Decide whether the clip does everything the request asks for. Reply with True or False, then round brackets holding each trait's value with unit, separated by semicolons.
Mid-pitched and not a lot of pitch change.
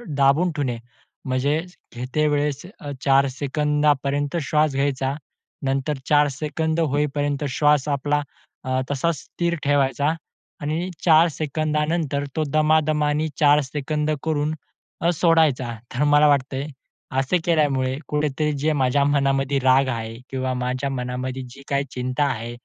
True (145 Hz; 2.2 semitones)